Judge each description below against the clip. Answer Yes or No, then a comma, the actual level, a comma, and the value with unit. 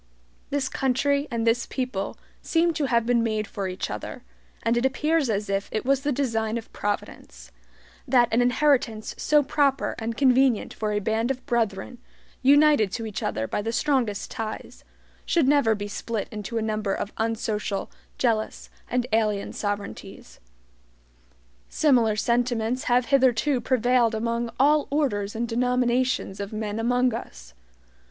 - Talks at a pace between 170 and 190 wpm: No, average, 150 wpm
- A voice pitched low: No, high, 235 Hz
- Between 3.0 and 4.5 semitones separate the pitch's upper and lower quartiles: Yes, average, 3.3 semitones